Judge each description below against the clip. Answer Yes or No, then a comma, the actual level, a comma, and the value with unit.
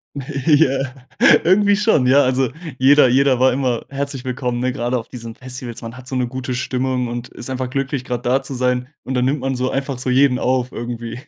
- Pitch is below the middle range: Yes, low, 130 Hz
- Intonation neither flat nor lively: No, narrow, 1.5 semitones